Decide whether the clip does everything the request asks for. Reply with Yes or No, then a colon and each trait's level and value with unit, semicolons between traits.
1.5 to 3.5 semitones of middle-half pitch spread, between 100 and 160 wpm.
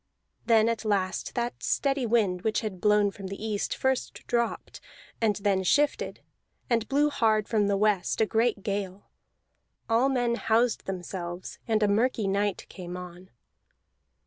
Yes: average, 3.1 semitones; average, 150 wpm